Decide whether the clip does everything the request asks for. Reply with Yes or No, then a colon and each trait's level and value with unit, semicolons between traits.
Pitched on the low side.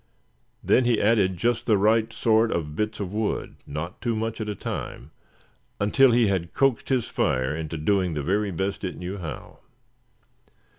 Yes: low, 100 Hz